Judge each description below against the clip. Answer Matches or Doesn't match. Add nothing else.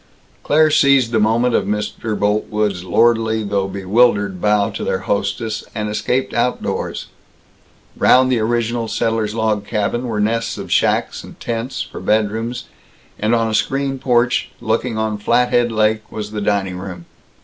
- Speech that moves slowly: Doesn't match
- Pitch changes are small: Matches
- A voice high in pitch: Doesn't match